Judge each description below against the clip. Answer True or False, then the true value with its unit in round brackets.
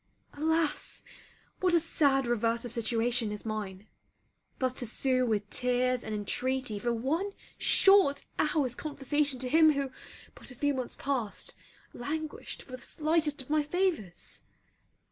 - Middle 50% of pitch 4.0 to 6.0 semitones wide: True (4.3 semitones)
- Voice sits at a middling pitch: False (260 Hz)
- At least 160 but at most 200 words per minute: False (145 wpm)